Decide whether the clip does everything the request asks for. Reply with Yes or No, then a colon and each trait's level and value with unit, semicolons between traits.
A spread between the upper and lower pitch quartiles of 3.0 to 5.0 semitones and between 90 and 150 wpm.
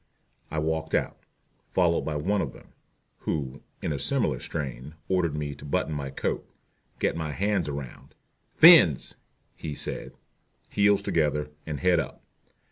Yes: average, 3.6 semitones; average, 145 wpm